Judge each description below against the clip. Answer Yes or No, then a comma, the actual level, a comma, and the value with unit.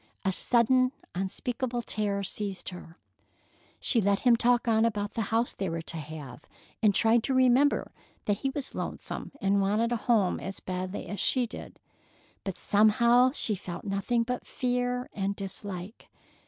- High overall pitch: Yes, high, 215 Hz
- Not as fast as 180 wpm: Yes, average, 160 wpm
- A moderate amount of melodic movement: Yes, average, 3.9 semitones